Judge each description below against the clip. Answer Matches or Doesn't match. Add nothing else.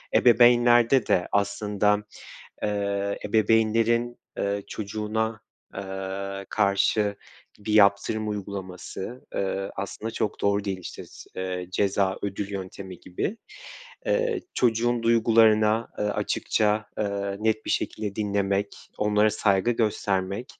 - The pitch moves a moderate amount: Doesn't match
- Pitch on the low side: Matches